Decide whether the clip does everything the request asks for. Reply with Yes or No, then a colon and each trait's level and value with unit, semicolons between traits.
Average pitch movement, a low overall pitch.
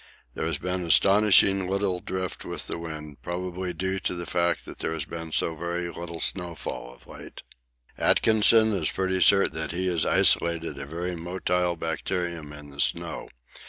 No: narrow, 2.1 semitones; very low, 85 Hz